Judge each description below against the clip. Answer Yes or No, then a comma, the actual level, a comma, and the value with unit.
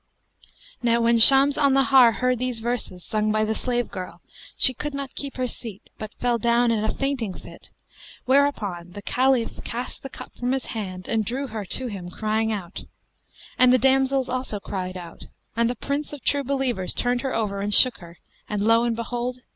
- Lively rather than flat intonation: No, average, 3.5 semitones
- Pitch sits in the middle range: No, high, 235 Hz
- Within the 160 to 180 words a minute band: No, average, 195 wpm